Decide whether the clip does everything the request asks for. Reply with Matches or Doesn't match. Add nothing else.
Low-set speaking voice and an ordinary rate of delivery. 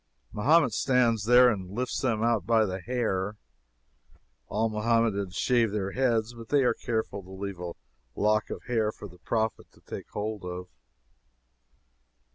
Matches